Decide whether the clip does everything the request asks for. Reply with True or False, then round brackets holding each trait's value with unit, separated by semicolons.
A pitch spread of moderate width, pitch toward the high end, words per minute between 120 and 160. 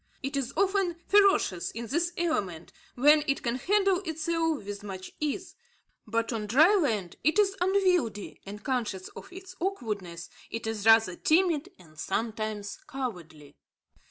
False (8.9 semitones; 255 Hz; 145 wpm)